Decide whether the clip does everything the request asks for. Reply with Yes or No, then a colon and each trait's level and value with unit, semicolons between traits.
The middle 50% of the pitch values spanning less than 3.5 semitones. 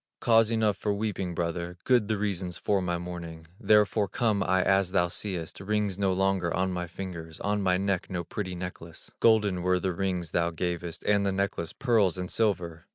Yes: average, 2.7 semitones